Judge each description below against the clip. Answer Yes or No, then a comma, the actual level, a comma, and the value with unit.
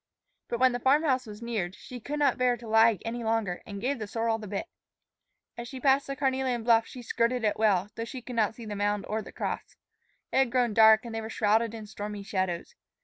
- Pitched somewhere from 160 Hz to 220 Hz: No, high, 230 Hz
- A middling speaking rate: No, fast, 240 wpm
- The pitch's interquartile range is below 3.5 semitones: Yes, average, 2.9 semitones